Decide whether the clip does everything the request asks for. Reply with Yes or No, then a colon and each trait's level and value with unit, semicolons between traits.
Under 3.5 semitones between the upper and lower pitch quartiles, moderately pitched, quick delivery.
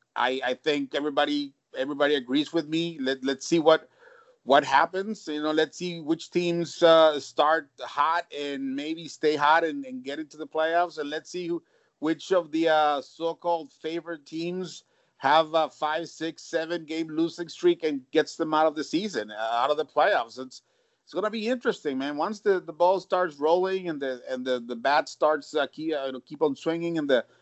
No: average, 2.7 semitones; medium, 160 Hz; average, 195 wpm